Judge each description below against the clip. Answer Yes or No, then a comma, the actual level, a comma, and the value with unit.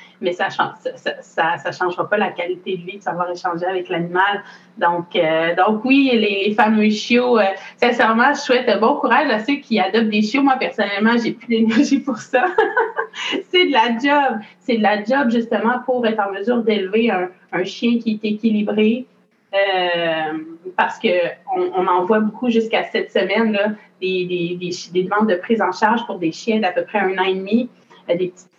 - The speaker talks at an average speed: Yes, average, 205 wpm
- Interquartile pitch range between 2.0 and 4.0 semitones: No, average, 4.7 semitones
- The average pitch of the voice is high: Yes, high, 215 Hz